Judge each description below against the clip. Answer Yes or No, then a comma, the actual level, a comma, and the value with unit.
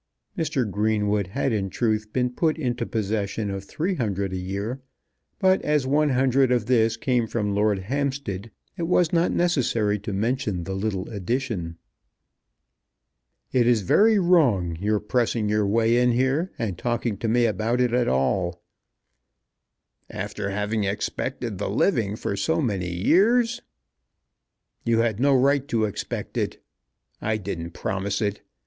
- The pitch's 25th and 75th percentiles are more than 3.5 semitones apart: Yes, average, 4.6 semitones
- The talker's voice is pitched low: Yes, low, 110 Hz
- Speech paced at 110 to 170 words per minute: Yes, average, 150 wpm